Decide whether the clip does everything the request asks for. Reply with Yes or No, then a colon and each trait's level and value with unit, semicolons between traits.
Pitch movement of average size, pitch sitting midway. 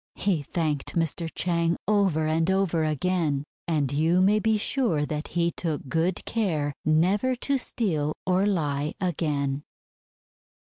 Yes: average, 3.9 semitones; medium, 165 Hz